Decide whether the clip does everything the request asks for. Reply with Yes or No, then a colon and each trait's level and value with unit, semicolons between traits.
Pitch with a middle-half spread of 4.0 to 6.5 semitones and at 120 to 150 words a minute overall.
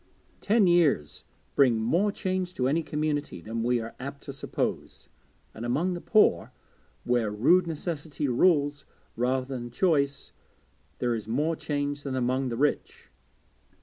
Yes: average, 4.8 semitones; average, 145 wpm